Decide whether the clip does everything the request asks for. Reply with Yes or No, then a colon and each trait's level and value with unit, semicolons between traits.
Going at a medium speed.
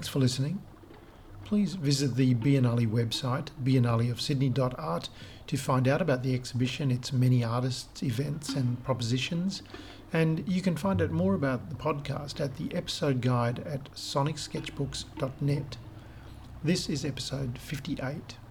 No: slow, 130 wpm